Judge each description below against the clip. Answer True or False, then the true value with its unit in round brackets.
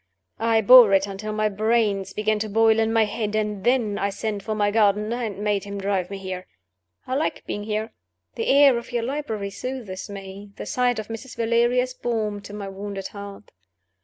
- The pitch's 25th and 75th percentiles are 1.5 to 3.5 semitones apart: True (2.4 semitones)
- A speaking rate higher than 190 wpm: True (200 wpm)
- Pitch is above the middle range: True (215 Hz)